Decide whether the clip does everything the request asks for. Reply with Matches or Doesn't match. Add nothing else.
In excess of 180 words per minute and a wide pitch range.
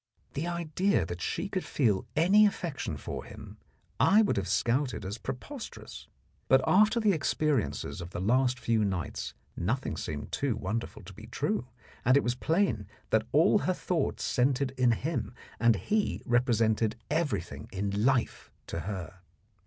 Doesn't match